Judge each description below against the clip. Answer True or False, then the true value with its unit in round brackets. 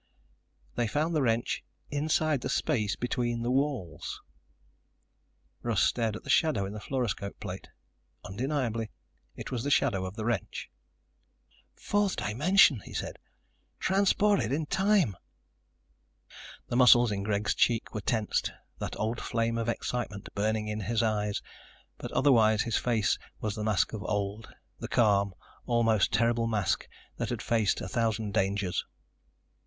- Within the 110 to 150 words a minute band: True (140 wpm)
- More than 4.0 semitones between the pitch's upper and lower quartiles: False (3.3 semitones)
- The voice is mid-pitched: False (115 Hz)